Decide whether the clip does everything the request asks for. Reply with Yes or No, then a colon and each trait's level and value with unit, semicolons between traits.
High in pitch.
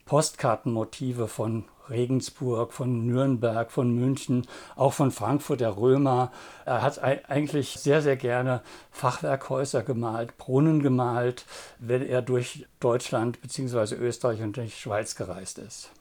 No: low, 125 Hz